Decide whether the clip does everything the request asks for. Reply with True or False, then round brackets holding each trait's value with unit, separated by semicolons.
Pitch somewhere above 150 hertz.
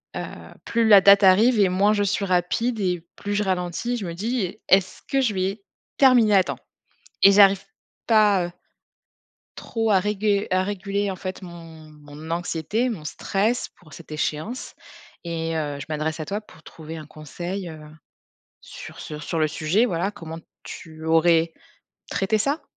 True (185 Hz)